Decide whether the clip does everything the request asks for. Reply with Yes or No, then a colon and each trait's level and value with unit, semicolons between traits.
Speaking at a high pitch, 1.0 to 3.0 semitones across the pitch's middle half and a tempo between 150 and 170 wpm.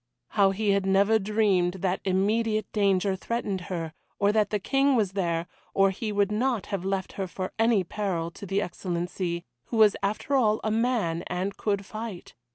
No: high, 200 Hz; narrow, 2.5 semitones; average, 180 wpm